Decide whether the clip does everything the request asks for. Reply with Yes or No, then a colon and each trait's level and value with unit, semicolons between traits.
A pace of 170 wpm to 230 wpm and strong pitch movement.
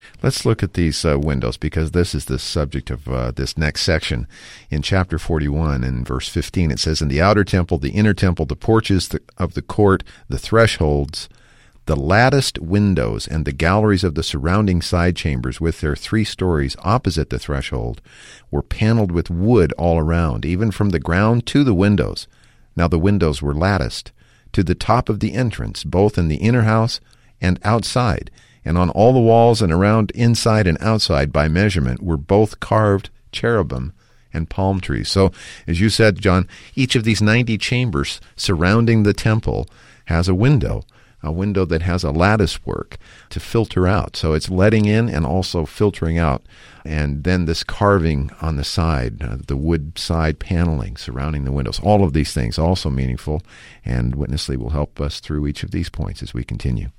Yes: average, 180 wpm; wide, 5.7 semitones